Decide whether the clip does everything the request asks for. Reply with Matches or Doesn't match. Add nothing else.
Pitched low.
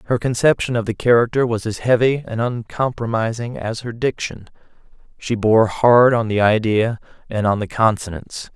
Matches